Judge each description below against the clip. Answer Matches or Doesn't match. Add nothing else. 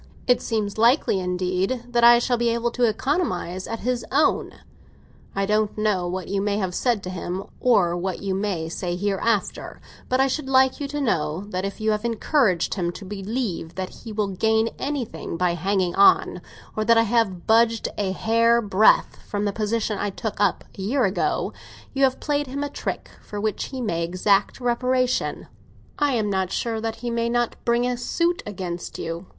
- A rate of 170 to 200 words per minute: Matches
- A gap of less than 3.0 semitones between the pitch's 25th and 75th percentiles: Doesn't match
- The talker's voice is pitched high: Matches